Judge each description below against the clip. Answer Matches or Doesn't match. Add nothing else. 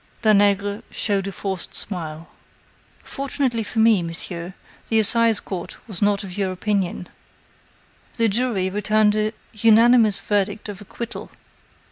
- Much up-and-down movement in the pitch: Doesn't match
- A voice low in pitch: Doesn't match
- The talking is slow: Matches